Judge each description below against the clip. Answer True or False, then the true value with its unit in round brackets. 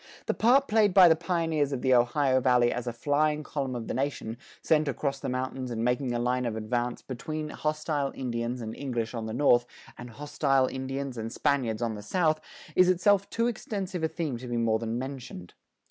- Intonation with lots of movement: False (4.3 semitones)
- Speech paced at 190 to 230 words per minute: True (205 wpm)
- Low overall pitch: True (130 Hz)